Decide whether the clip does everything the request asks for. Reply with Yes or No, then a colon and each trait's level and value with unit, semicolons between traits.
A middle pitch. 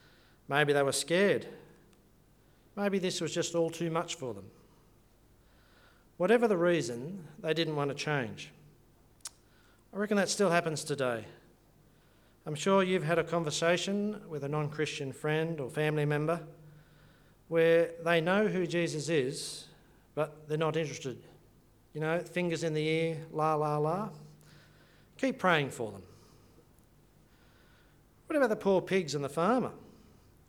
Yes: medium, 160 Hz